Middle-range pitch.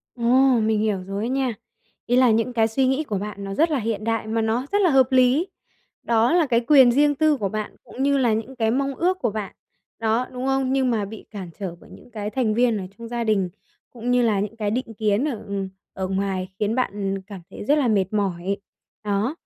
No: high, 225 Hz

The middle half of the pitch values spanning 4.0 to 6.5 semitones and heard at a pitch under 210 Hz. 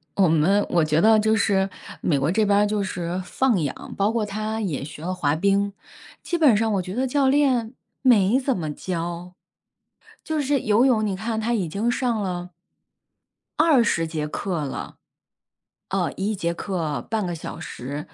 Yes: average, 4.6 semitones; high, 200 Hz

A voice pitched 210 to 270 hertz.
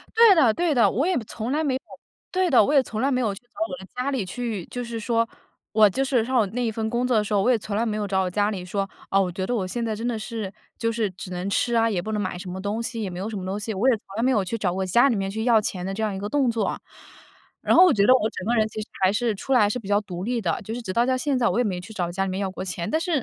Yes: high, 220 Hz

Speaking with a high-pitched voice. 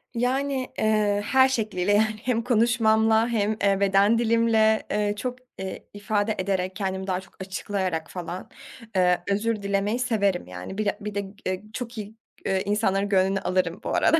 Yes: high, 205 Hz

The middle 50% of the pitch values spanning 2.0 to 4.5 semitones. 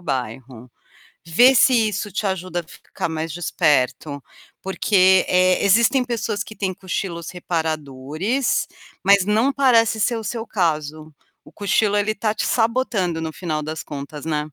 No: wide, 5.6 semitones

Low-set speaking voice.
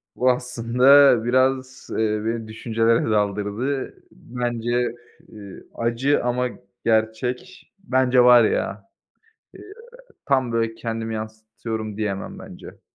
Yes: low, 115 Hz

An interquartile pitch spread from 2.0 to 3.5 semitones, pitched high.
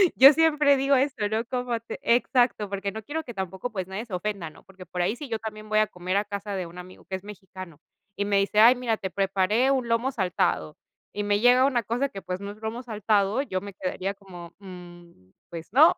No: average, 4.3 semitones; high, 205 Hz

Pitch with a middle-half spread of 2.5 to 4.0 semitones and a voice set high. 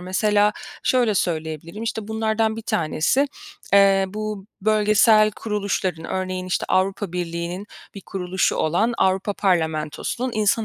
Yes: average, 3.1 semitones; high, 195 Hz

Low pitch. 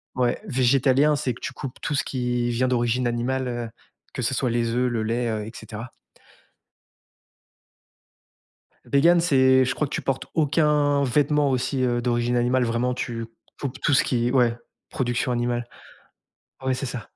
Yes: low, 125 Hz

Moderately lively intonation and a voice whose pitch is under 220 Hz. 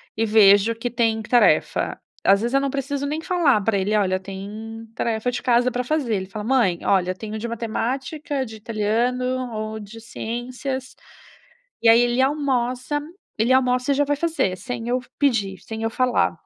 No: average, 3.1 semitones; high, 235 Hz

